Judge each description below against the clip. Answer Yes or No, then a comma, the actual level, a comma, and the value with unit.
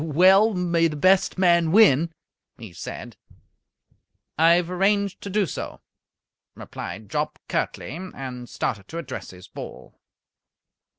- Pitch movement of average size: No, wide, 5.8 semitones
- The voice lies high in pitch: No, medium, 170 Hz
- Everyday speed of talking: No, slow, 125 wpm